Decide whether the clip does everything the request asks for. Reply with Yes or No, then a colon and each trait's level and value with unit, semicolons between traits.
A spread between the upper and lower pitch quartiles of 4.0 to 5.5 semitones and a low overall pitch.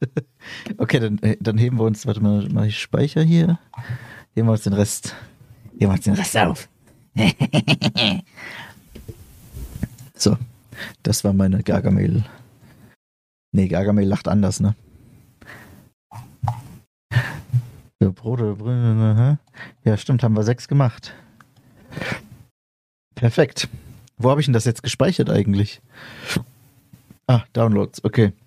No: average, 3.3 semitones; low, 115 Hz